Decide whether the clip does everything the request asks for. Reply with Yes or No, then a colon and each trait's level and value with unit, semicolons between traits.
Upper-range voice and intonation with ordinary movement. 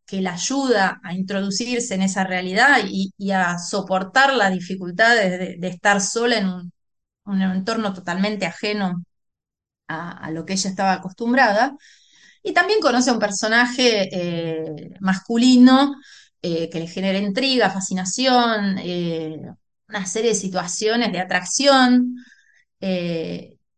Yes: high, 195 Hz; average, 4.3 semitones